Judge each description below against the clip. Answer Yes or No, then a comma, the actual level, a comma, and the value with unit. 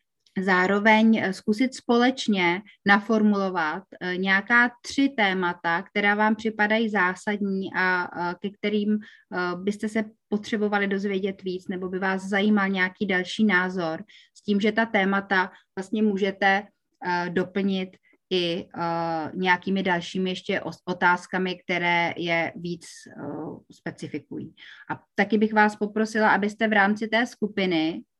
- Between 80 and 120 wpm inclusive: Yes, slow, 115 wpm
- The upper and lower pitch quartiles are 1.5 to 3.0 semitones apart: Yes, average, 2.7 semitones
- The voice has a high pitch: Yes, high, 195 Hz